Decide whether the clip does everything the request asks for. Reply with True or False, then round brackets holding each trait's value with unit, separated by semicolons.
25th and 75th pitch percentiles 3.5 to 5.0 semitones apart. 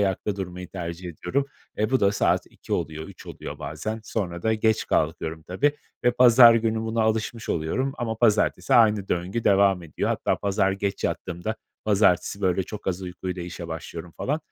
True (4.1 semitones)